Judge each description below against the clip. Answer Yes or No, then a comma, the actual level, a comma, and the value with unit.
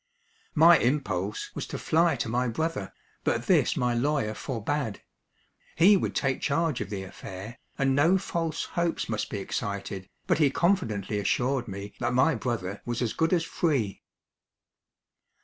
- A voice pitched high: No, low, 125 Hz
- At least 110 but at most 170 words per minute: Yes, average, 155 wpm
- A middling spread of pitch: No, wide, 7.3 semitones